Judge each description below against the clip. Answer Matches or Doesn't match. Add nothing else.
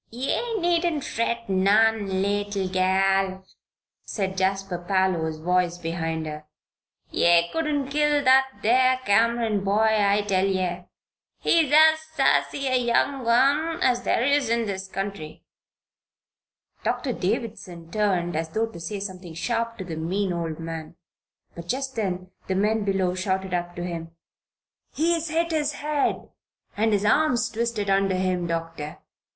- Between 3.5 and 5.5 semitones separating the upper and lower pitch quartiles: Matches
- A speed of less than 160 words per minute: Matches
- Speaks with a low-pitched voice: Doesn't match